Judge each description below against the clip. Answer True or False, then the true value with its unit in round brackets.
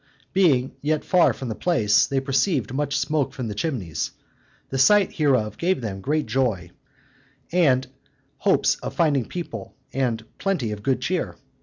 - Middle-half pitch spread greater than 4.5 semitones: True (5.6 semitones)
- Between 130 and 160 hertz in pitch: True (135 Hz)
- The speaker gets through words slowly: False (155 wpm)